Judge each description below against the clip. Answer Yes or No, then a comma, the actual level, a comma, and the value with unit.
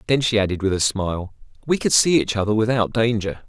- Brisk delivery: Yes, fast, 225 wpm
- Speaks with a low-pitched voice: Yes, low, 110 Hz